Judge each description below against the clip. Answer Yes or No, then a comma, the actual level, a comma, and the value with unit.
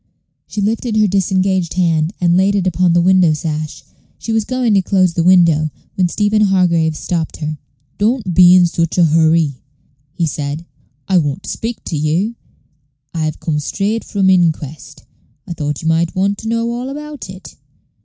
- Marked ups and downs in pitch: No, average, 3.8 semitones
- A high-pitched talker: No, medium, 180 Hz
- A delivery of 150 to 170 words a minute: No, average, 180 wpm